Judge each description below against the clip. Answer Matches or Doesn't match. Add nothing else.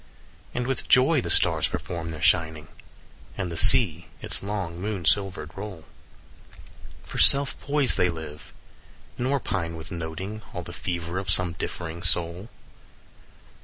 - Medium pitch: Doesn't match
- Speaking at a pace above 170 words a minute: Doesn't match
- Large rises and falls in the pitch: Doesn't match